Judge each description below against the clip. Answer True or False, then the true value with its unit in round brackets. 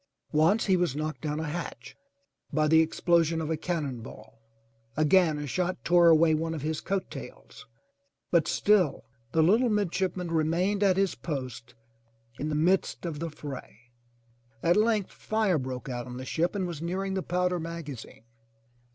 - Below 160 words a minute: False (175 wpm)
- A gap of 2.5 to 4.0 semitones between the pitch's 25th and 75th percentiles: True (3.4 semitones)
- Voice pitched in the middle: True (165 Hz)